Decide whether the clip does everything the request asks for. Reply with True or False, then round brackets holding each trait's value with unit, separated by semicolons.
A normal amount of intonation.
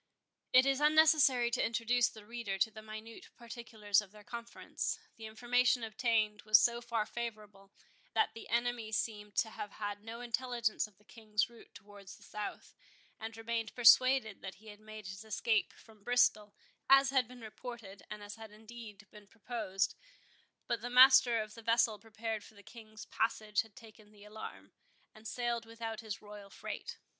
False (2.1 semitones)